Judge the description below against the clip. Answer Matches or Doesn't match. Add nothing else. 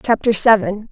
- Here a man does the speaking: Doesn't match